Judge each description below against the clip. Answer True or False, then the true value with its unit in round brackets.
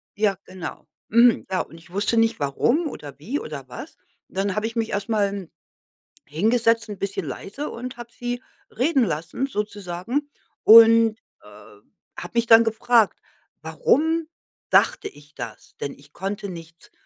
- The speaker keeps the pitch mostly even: False (4.4 semitones)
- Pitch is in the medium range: False (215 Hz)